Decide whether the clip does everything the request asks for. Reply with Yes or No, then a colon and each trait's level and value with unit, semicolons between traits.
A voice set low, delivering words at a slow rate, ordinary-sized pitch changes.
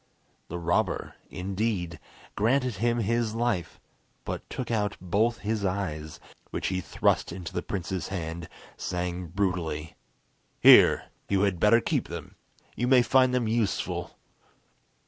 Yes: low, 100 Hz; slow, 130 wpm; average, 4.8 semitones